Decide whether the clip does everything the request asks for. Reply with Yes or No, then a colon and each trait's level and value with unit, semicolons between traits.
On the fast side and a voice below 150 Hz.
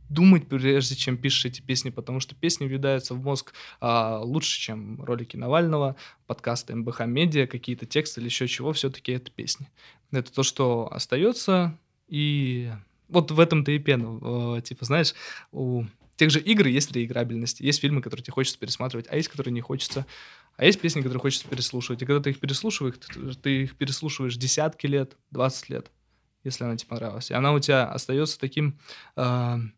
Yes: fast, 170 wpm; low, 135 Hz